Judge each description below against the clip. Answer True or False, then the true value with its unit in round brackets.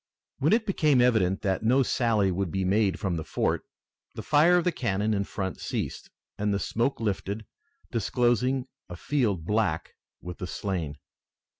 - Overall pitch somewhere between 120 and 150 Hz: False (105 Hz)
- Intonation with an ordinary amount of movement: True (4.7 semitones)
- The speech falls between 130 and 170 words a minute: True (165 wpm)